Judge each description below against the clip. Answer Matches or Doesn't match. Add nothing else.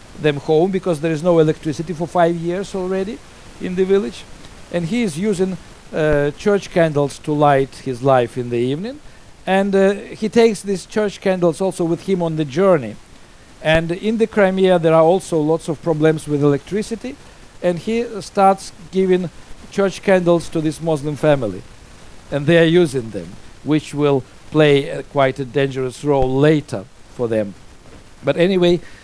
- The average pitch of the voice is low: Doesn't match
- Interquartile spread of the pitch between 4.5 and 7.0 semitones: Matches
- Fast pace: Doesn't match